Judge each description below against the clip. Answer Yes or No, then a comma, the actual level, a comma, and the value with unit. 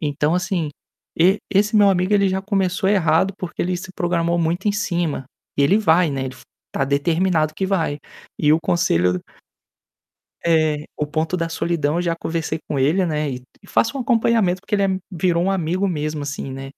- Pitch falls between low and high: Yes, medium, 170 Hz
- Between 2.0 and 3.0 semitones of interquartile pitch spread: No, average, 3.9 semitones